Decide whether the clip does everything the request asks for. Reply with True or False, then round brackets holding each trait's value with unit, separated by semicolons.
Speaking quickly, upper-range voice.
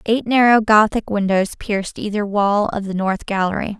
False (175 wpm; 205 Hz)